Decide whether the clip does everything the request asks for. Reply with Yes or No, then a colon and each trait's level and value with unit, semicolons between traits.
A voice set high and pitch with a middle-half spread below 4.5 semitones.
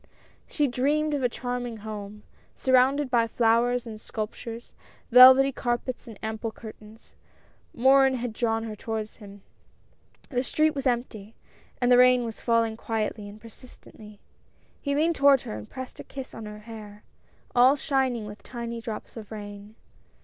Yes: high, 235 Hz; average, 3.0 semitones